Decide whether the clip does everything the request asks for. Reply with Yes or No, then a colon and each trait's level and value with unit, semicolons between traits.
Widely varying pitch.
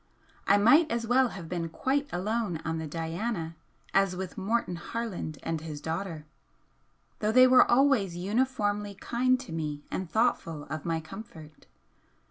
Yes: wide, 6.3 semitones